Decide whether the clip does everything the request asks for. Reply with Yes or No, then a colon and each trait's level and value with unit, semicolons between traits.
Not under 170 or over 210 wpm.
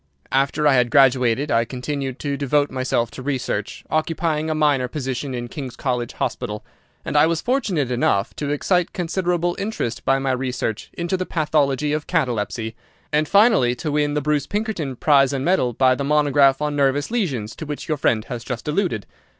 Yes: average, 185 wpm